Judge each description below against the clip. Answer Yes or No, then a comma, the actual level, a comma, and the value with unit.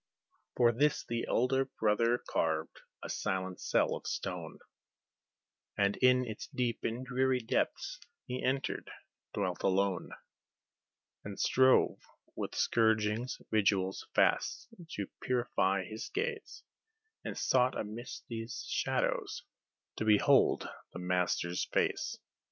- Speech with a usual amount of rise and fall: Yes, average, 4.3 semitones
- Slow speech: Yes, slow, 110 wpm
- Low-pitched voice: Yes, low, 115 Hz